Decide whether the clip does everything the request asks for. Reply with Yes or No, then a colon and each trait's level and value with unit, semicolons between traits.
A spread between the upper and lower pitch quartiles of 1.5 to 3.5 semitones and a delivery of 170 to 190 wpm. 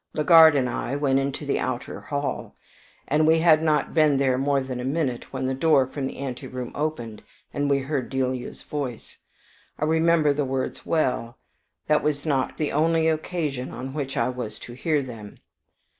Yes: average, 3.0 semitones; average, 180 wpm